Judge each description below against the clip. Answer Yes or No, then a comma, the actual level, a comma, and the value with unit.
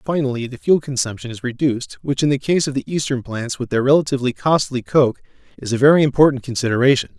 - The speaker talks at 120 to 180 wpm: No, average, 200 wpm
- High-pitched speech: No, low, 135 Hz